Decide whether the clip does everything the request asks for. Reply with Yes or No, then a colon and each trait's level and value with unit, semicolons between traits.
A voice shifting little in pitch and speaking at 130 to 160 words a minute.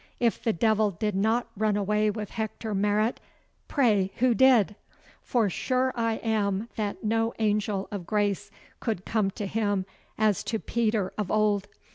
Yes: narrow, 1.8 semitones; average, 155 wpm